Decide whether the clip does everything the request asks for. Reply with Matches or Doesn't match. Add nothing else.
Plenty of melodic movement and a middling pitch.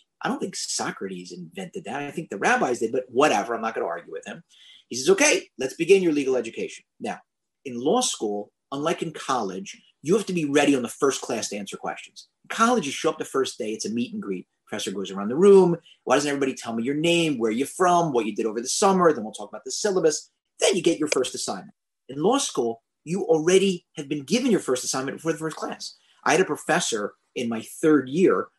Matches